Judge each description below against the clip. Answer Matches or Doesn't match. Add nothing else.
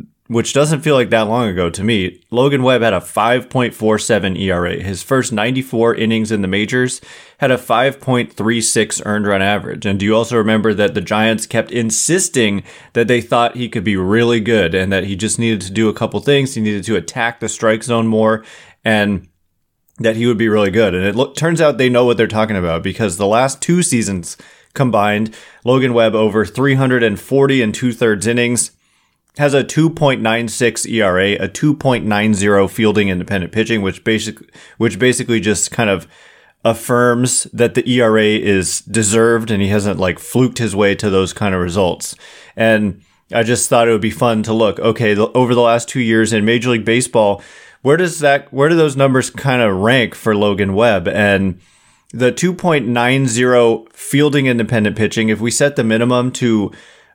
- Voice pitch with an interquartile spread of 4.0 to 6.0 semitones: Doesn't match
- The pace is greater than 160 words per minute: Matches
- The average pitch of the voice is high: Doesn't match